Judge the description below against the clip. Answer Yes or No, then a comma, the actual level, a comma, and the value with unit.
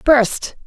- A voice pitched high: Yes, very high, 255 Hz